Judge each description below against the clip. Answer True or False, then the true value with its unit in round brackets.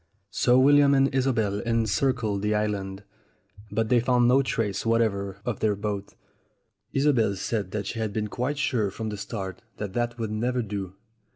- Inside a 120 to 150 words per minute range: False (165 wpm)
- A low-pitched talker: True (110 Hz)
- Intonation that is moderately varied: True (3.4 semitones)